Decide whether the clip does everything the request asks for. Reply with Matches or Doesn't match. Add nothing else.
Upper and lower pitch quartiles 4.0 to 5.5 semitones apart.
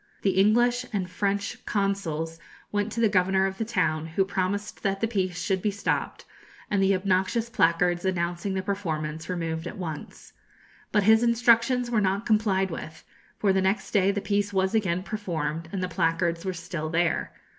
Doesn't match